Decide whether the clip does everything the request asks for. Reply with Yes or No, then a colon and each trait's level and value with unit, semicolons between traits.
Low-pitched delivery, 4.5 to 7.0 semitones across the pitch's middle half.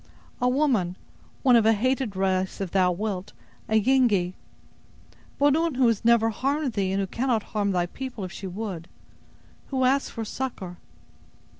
No: high, 220 Hz; average, 5.3 semitones